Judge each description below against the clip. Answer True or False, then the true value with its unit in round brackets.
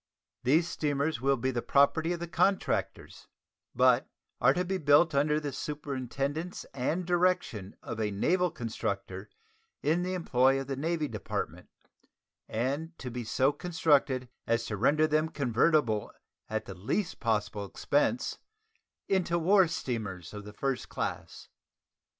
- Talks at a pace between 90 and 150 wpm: True (140 wpm)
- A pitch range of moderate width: False (5.8 semitones)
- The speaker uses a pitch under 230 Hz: True (140 Hz)